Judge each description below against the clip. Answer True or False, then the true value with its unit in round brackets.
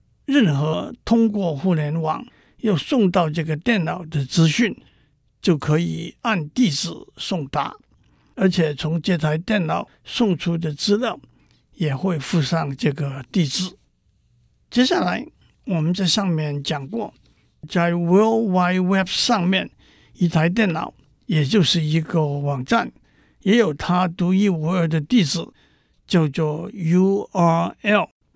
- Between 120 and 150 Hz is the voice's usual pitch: False (175 Hz)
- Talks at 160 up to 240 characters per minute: True (205 characters per minute)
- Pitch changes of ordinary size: True (3.9 semitones)